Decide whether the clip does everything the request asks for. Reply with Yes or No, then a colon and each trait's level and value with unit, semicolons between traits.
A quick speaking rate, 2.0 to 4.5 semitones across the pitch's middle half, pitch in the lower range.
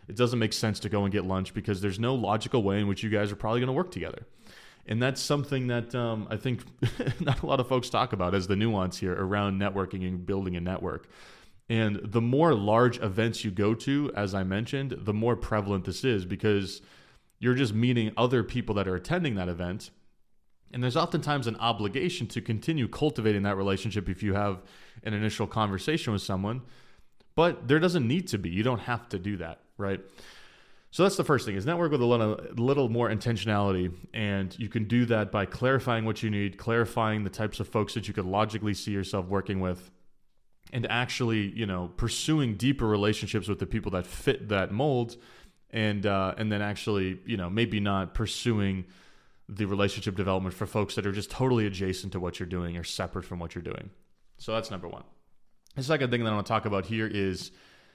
Yes: fast, 210 wpm; average, 3.4 semitones; low, 110 Hz